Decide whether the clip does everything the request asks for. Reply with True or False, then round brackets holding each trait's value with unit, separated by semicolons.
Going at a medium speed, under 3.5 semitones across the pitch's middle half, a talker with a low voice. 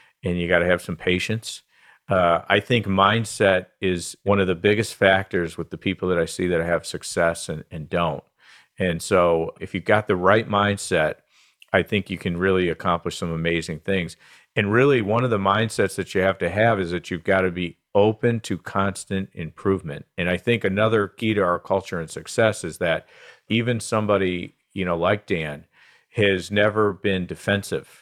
True (190 wpm; 2.9 semitones; 95 Hz)